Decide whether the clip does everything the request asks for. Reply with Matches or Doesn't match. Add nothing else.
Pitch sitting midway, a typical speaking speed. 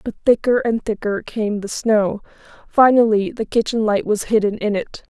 Doesn't match